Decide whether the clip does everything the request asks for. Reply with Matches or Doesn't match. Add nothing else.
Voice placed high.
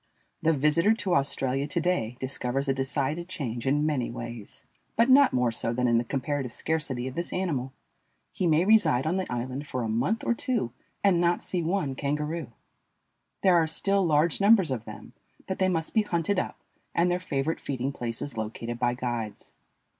Doesn't match